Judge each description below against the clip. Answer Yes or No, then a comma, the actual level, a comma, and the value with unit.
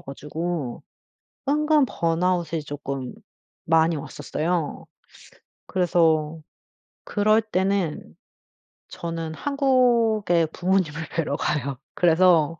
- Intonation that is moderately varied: Yes, average, 3.8 semitones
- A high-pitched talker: No, medium, 170 Hz